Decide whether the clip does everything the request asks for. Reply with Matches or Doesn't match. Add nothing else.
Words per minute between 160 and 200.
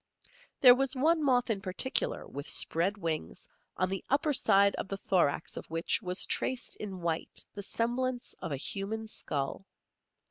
Matches